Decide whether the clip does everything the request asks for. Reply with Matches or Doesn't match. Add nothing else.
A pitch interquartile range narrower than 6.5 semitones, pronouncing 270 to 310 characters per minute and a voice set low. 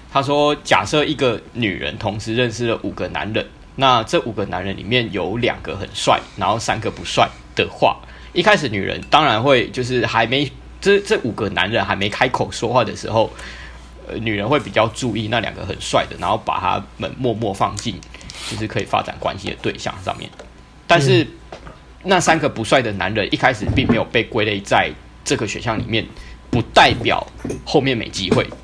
Matches